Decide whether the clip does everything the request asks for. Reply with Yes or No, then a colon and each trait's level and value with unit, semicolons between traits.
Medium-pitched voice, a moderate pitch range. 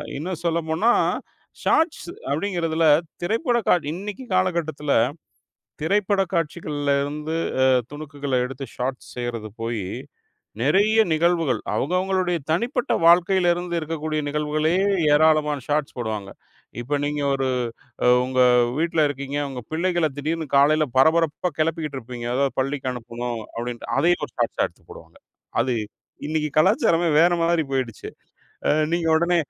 Yes: medium, 155 Hz; average, 4.0 semitones